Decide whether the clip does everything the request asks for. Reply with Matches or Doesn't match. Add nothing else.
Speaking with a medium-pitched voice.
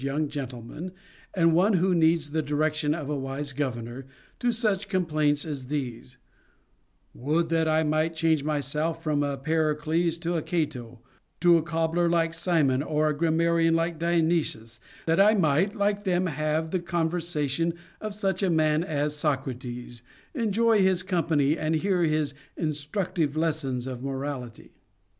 Matches